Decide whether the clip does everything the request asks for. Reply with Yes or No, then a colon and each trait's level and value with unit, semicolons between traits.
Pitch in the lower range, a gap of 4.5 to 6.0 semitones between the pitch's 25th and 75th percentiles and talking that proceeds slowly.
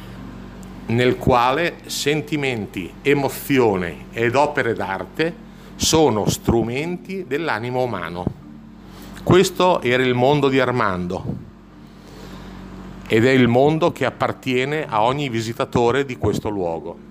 Yes: low, 130 Hz; average, 4.8 semitones; slow, 100 wpm